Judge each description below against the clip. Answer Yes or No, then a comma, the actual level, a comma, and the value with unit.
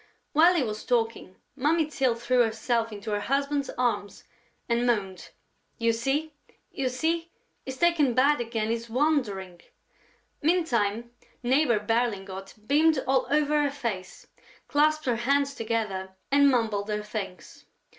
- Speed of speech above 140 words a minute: No, slow, 135 wpm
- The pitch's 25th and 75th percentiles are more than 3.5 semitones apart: Yes, average, 4.8 semitones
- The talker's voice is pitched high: Yes, high, 240 Hz